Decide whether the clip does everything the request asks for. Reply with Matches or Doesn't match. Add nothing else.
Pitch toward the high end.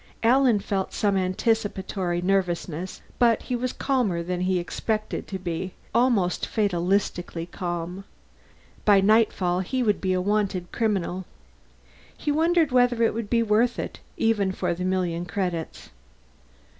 Matches